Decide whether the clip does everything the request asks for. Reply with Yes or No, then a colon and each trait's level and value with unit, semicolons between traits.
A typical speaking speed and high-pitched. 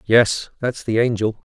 No: average, 160 wpm; low, 115 Hz